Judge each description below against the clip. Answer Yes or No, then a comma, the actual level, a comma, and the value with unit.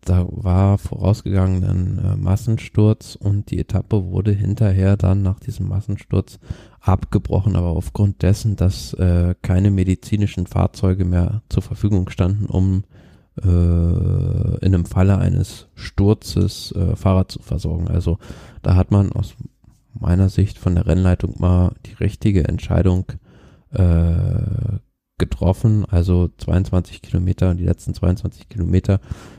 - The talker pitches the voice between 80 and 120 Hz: Yes, very low, 95 Hz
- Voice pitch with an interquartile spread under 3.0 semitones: Yes, narrow, 2.4 semitones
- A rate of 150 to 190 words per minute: No, slow, 125 wpm